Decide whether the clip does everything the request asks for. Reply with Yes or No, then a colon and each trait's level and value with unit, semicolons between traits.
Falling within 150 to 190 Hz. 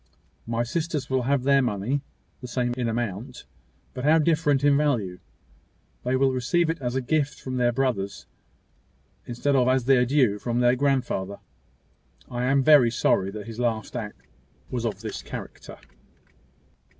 No: low, 125 Hz